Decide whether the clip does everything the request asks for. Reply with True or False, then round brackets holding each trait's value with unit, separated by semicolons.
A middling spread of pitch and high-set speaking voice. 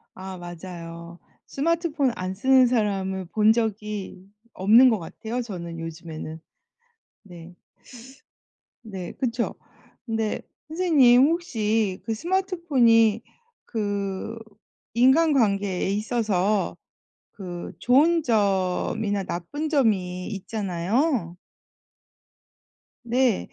True (5.0 semitones; 215 Hz)